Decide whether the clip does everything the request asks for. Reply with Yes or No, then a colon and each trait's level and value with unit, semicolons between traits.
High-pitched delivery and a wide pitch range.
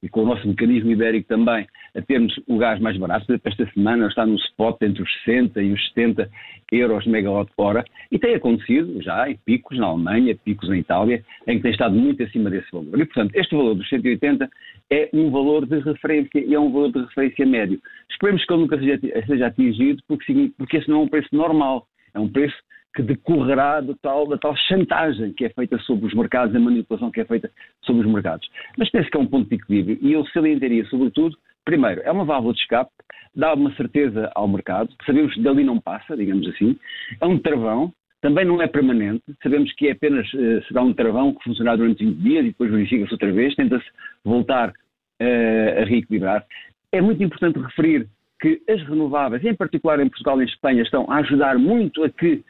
No: medium, 140 Hz; wide, 7.5 semitones